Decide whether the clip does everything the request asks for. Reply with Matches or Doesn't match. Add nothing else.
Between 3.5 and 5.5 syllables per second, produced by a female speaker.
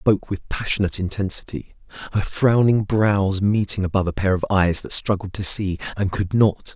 Doesn't match